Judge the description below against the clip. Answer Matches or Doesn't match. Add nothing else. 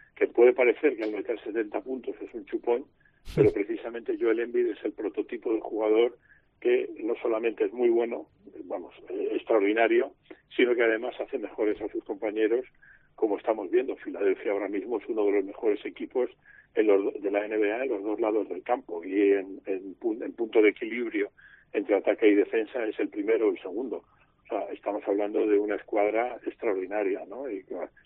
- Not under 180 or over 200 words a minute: Matches